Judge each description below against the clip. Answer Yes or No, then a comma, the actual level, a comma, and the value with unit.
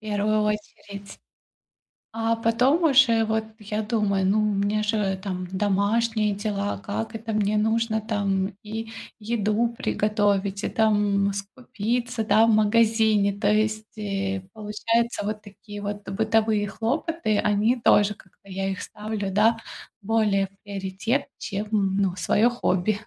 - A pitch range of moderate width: No, narrow, 1.8 semitones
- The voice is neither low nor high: No, high, 210 Hz